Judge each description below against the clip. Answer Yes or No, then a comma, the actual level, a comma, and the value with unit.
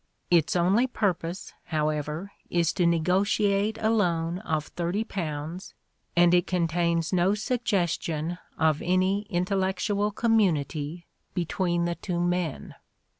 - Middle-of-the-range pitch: Yes, medium, 175 Hz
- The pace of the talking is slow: Yes, slow, 110 wpm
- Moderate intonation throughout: Yes, average, 3.1 semitones